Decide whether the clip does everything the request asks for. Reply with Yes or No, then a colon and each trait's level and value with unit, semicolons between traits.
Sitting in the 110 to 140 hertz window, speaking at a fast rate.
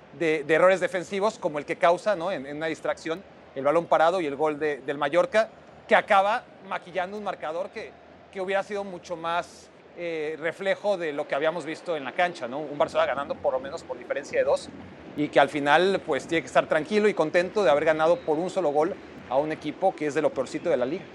No: medium, 170 Hz; fast, 235 wpm